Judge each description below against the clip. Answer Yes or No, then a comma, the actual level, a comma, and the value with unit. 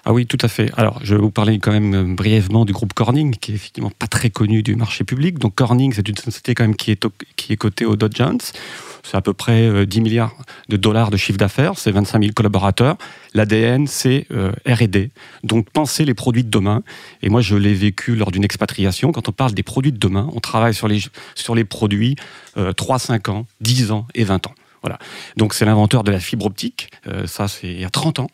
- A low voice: Yes, low, 110 Hz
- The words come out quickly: Yes, fast, 230 wpm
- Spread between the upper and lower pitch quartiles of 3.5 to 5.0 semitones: No, average, 2.8 semitones